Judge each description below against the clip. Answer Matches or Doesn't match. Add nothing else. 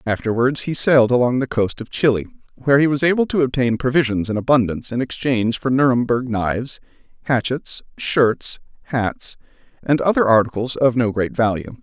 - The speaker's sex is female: Doesn't match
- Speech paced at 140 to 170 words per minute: Matches